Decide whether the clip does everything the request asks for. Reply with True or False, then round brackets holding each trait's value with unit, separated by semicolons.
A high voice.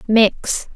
True (220 Hz)